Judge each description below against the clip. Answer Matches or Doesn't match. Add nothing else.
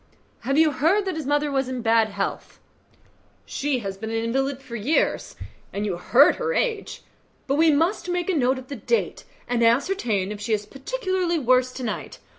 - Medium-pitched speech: Doesn't match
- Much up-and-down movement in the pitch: Matches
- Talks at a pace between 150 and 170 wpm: Doesn't match